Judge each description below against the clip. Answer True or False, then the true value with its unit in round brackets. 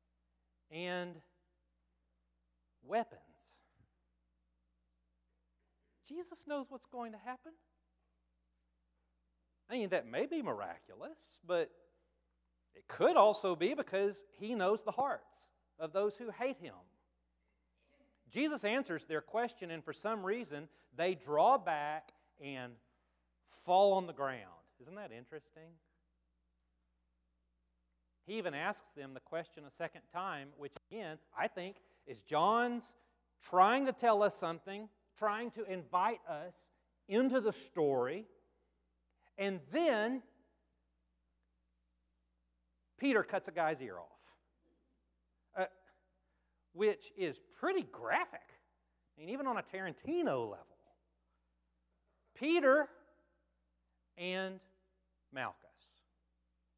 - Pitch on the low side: False (155 Hz)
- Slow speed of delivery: True (105 wpm)